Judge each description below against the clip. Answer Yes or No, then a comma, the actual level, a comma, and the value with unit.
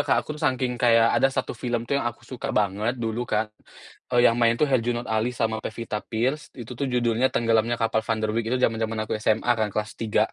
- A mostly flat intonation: Yes, narrow, 1.7 semitones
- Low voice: Yes, low, 115 Hz